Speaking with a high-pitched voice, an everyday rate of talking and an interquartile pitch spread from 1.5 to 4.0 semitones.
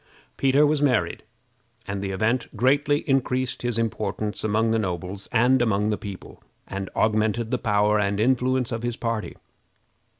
No: low, 110 Hz; average, 155 wpm; average, 3.7 semitones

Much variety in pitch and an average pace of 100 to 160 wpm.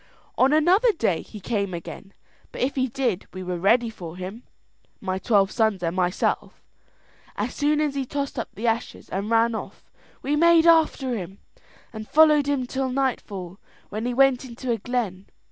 No: wide, 5.7 semitones; average, 180 wpm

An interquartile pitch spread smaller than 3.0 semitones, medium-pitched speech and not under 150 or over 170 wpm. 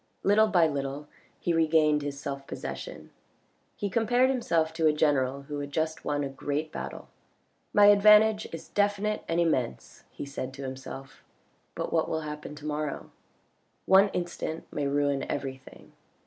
No: average, 5.2 semitones; medium, 155 Hz; average, 160 wpm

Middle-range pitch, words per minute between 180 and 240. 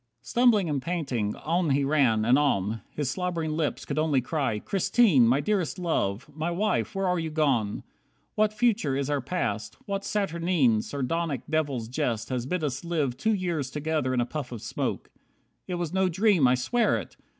Yes: medium, 150 Hz; average, 185 wpm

